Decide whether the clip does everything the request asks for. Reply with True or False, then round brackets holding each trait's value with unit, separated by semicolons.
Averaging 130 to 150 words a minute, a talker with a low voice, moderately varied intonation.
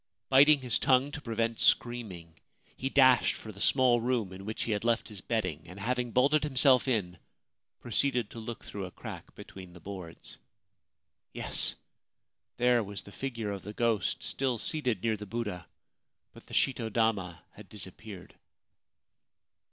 False (160 wpm; 115 Hz; 4.1 semitones)